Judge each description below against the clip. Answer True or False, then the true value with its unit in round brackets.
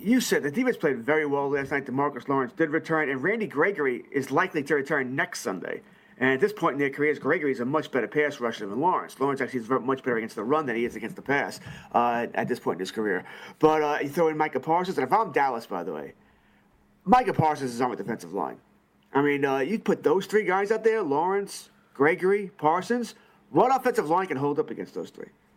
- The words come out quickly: True (240 wpm)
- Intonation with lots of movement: True (6.0 semitones)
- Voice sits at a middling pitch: True (150 Hz)